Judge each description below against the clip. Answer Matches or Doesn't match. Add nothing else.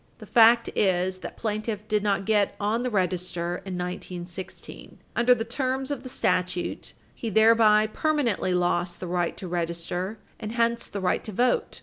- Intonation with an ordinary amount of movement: Matches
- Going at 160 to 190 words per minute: Matches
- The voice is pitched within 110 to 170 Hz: Doesn't match